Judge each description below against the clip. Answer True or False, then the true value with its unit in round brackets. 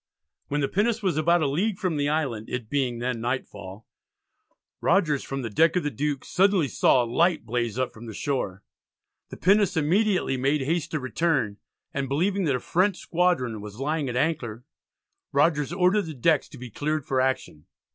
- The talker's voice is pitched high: False (145 Hz)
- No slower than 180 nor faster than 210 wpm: True (185 wpm)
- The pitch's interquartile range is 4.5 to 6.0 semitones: True (5.4 semitones)